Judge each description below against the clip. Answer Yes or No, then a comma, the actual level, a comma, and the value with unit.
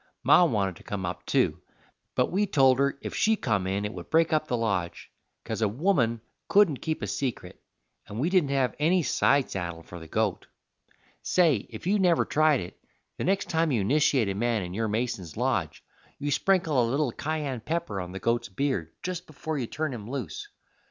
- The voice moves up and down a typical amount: No, wide, 7.5 semitones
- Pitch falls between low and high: No, low, 130 Hz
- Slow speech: No, average, 200 wpm